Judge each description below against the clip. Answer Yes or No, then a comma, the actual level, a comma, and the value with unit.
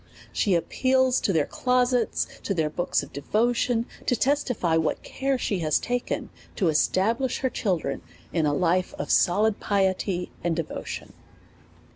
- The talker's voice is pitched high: Yes, high, 200 Hz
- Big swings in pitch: Yes, wide, 6.4 semitones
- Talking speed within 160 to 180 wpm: No, average, 150 wpm